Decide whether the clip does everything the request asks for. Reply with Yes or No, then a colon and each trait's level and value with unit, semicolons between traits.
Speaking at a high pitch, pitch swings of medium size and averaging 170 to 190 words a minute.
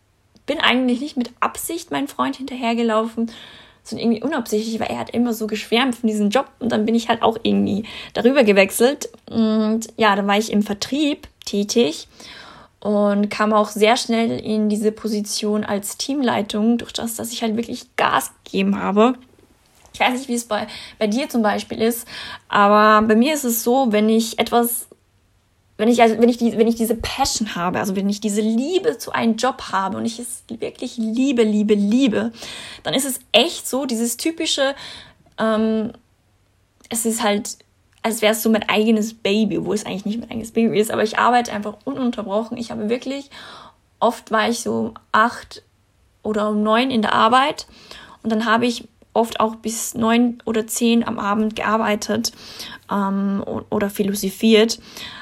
No: high, 225 Hz; narrow, 2.1 semitones; average, 180 wpm